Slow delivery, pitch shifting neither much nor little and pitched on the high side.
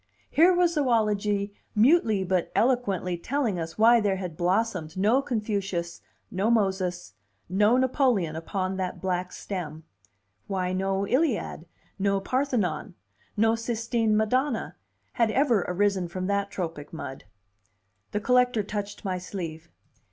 Yes: slow, 125 wpm; average, 4.1 semitones; high, 200 Hz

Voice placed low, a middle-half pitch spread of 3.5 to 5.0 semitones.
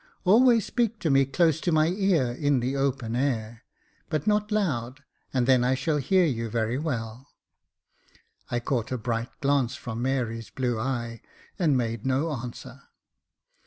Yes: low, 130 Hz; average, 4.7 semitones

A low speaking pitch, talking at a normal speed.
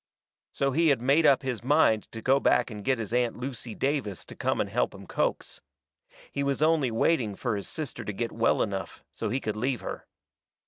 No: low, 125 Hz; fast, 215 wpm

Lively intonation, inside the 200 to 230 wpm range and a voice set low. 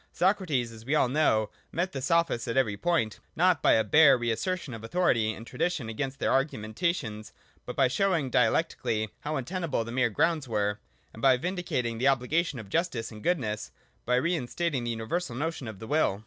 Yes: wide, 6.8 semitones; fast, 205 wpm; low, 130 Hz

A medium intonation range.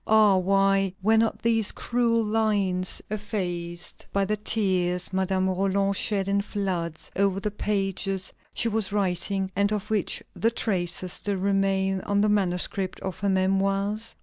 No: narrow, 1.8 semitones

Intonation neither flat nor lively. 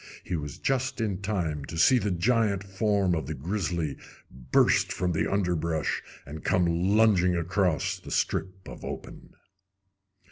Yes: average, 3.7 semitones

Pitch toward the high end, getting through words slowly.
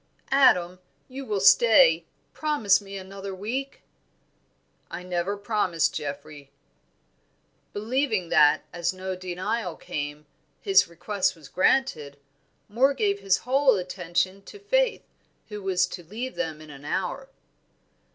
Yes: high, 195 Hz; slow, 120 wpm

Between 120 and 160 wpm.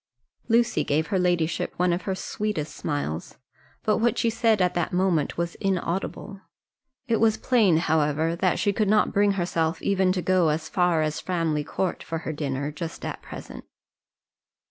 No: average, 170 wpm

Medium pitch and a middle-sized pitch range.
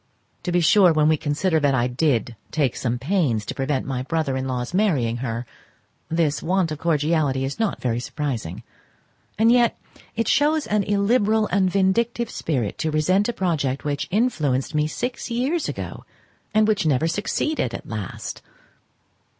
No: medium, 155 Hz; wide, 7.3 semitones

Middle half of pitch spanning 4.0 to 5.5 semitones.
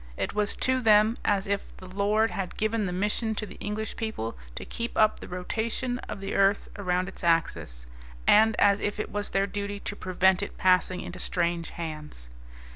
No: average, 2.8 semitones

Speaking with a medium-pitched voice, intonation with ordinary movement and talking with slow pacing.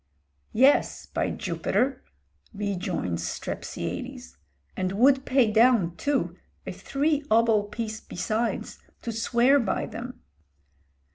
No: high, 230 Hz; average, 4.3 semitones; slow, 100 wpm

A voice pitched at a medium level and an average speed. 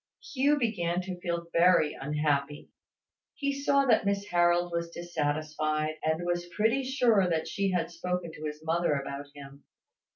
Yes: medium, 175 Hz; average, 155 wpm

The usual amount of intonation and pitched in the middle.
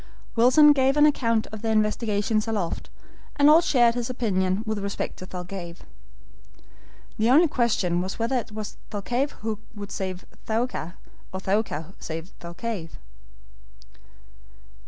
No: average, 4.2 semitones; high, 215 Hz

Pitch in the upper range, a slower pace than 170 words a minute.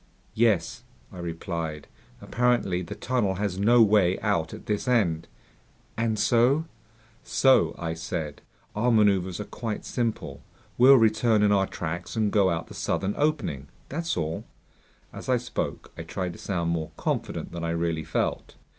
No: low, 100 Hz; average, 160 wpm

